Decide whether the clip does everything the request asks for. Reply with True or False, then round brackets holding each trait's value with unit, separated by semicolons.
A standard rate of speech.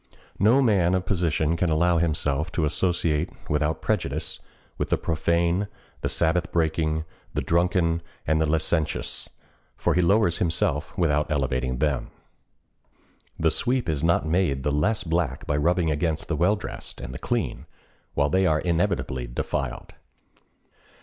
True (145 wpm)